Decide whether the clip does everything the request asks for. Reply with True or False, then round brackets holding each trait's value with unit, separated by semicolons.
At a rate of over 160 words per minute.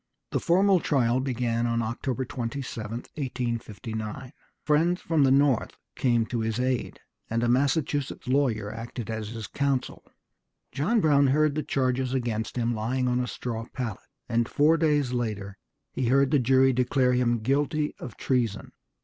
False (155 wpm)